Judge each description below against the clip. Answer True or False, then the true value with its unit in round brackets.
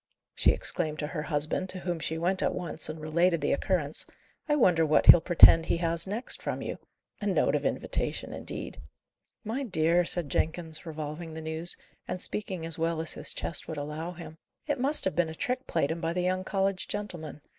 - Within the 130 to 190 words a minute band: False (205 wpm)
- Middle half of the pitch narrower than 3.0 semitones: True (2.6 semitones)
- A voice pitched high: False (170 Hz)